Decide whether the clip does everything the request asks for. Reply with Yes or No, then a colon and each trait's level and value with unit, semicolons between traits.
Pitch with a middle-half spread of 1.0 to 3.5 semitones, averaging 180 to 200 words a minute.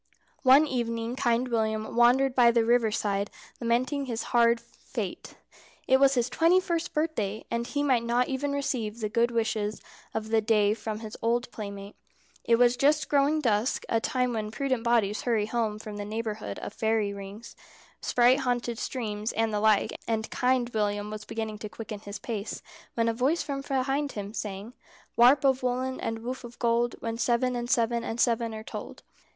Yes: narrow, 2.6 semitones; average, 185 wpm